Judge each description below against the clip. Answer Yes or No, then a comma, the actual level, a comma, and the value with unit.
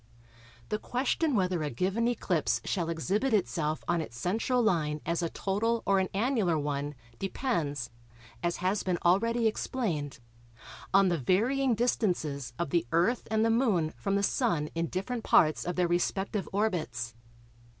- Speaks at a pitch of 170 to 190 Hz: Yes, medium, 185 Hz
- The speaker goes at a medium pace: Yes, average, 155 wpm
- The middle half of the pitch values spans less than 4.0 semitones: No, wide, 5.5 semitones